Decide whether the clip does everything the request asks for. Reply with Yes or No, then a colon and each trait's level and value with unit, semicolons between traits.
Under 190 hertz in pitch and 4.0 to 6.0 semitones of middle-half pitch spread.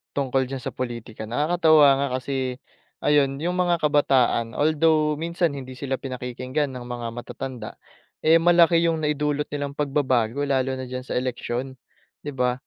No: low, 135 Hz; average, 3.0 semitones